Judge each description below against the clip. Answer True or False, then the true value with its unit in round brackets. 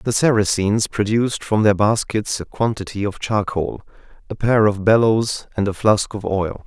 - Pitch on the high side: False (105 Hz)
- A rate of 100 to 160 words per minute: False (170 wpm)